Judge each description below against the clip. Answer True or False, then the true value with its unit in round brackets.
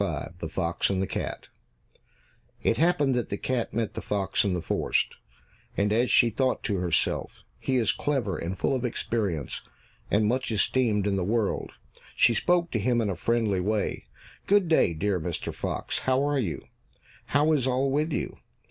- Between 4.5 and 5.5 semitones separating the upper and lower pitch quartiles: True (5.1 semitones)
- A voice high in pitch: False (115 Hz)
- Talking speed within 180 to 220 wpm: True (185 wpm)